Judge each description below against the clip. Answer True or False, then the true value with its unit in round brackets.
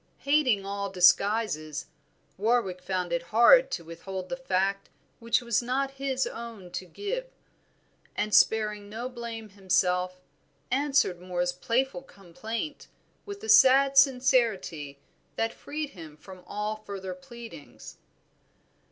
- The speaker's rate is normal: False (125 wpm)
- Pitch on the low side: False (215 Hz)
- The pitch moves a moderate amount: False (6.0 semitones)